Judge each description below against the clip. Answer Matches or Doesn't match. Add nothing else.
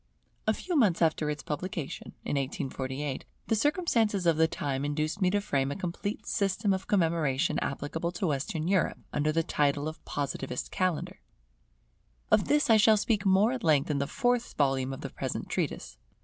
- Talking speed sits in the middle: Matches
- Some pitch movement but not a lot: Doesn't match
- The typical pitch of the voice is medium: Matches